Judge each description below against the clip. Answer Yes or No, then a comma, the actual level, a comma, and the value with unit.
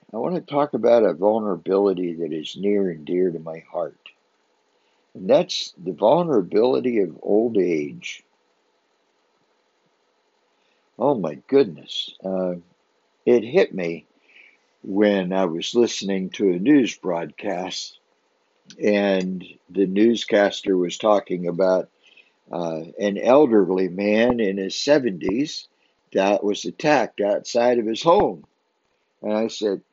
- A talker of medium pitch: No, low, 100 Hz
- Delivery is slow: Yes, slow, 120 wpm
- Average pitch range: Yes, average, 4.3 semitones